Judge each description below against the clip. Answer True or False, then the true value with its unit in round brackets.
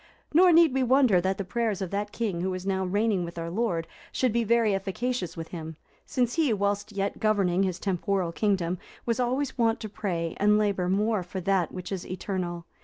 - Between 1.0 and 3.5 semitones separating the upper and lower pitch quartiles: False (4.1 semitones)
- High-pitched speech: True (200 Hz)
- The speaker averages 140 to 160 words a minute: False (205 wpm)